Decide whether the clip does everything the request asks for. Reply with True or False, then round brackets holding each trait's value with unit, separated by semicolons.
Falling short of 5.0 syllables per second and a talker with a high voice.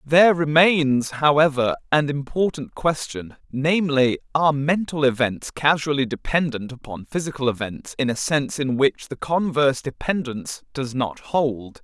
False (4.7 syllables/s; 140 Hz)